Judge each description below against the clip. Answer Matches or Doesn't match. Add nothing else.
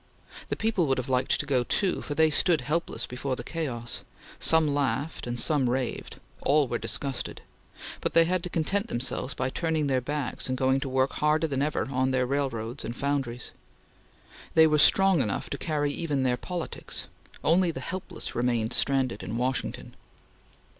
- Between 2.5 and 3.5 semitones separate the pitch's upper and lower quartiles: Doesn't match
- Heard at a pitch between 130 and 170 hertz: Matches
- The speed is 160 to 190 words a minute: Matches